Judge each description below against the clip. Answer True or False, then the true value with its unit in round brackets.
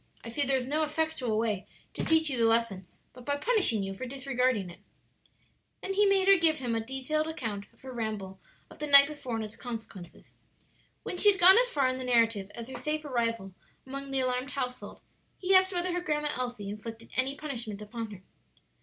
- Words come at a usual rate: False (210 wpm)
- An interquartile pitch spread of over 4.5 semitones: True (5.1 semitones)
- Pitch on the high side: True (255 Hz)